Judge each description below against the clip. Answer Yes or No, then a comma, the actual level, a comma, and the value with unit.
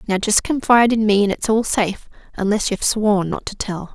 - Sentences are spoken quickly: Yes, fast, 230 wpm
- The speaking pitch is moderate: No, high, 210 Hz